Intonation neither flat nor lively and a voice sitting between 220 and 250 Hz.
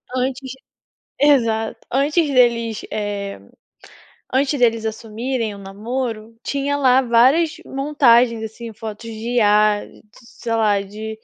Yes: average, 3.3 semitones; high, 230 Hz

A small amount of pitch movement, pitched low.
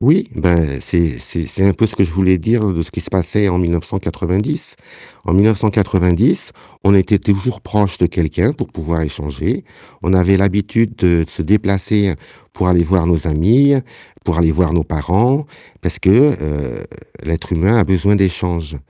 No: average, 3.4 semitones; very low, 90 Hz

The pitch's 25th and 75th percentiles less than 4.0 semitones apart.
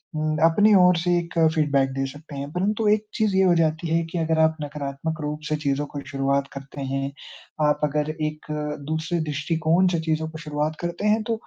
Yes: average, 2.7 semitones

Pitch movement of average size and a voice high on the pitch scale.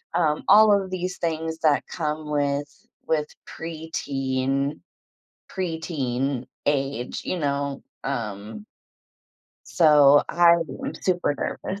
No: average, 3.5 semitones; medium, 150 Hz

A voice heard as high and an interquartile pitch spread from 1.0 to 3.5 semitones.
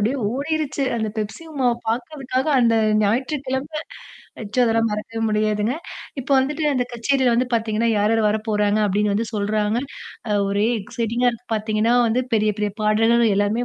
Yes: high, 225 Hz; average, 3.0 semitones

